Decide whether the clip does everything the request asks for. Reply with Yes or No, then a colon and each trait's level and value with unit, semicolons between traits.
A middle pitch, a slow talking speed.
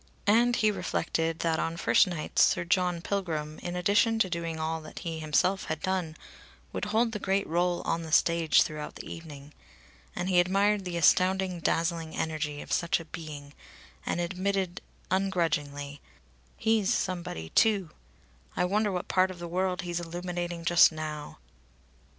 No: medium, 175 Hz; average, 160 wpm